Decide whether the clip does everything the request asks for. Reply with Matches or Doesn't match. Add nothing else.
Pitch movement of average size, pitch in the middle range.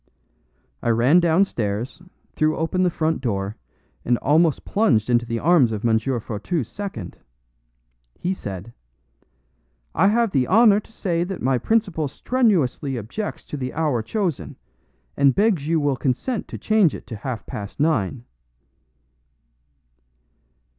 Doesn't match